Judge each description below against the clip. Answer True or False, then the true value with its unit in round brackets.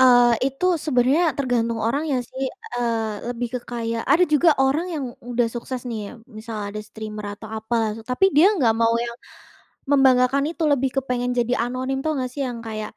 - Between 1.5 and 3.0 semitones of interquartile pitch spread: True (2.7 semitones)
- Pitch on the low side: False (245 Hz)